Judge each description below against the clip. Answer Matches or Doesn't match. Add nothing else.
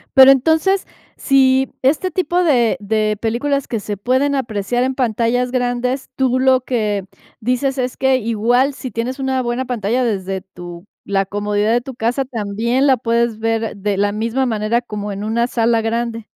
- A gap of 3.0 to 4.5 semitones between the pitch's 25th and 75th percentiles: Matches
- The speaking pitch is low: Doesn't match